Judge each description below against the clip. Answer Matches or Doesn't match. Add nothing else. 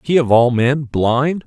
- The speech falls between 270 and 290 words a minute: Doesn't match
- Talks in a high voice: Doesn't match